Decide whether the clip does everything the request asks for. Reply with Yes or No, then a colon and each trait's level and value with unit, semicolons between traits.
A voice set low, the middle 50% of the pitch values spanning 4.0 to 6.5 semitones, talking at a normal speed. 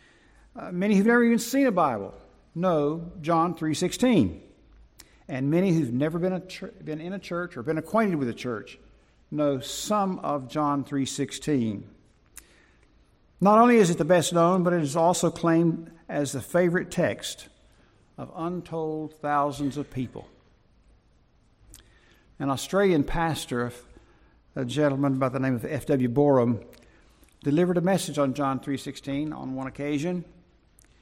No: medium, 150 Hz; average, 4.4 semitones; average, 145 wpm